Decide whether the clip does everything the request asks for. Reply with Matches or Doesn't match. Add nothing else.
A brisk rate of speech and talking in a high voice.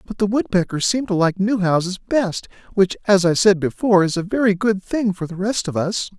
Matches